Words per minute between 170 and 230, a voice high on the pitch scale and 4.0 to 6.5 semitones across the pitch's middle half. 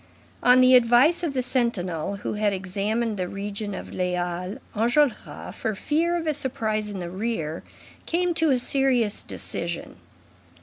No: average, 160 wpm; high, 220 Hz; average, 5.1 semitones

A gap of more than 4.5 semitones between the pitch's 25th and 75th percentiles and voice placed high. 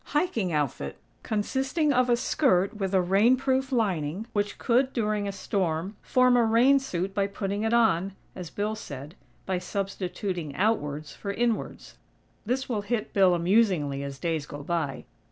Yes: wide, 5.4 semitones; high, 200 Hz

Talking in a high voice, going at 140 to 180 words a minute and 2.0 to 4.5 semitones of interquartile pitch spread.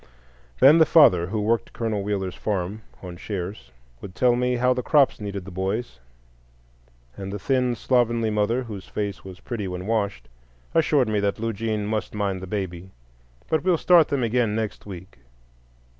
No: low, 105 Hz; average, 170 wpm; average, 4.0 semitones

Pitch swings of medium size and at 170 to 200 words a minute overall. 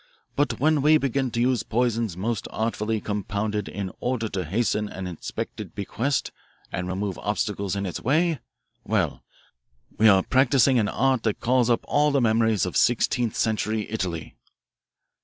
No: average, 3.9 semitones; average, 155 wpm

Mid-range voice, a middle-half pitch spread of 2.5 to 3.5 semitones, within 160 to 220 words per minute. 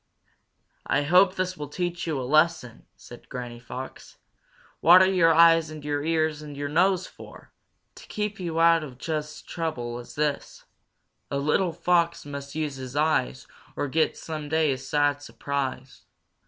Yes: medium, 155 Hz; average, 3.0 semitones; average, 165 wpm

